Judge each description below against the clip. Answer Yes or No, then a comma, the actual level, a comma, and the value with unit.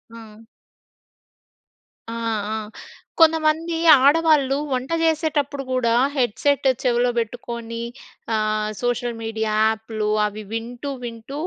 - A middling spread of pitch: Yes, average, 4.2 semitones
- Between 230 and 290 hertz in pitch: Yes, high, 245 Hz